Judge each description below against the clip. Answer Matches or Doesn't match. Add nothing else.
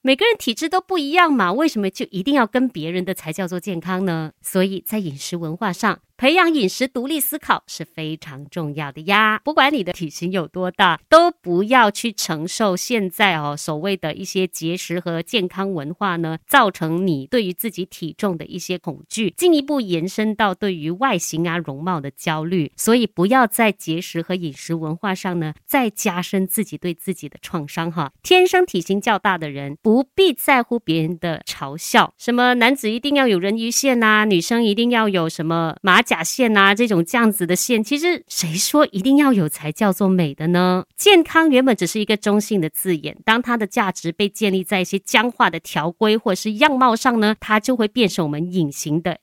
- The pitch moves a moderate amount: Doesn't match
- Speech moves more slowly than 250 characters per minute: Doesn't match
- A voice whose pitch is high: Matches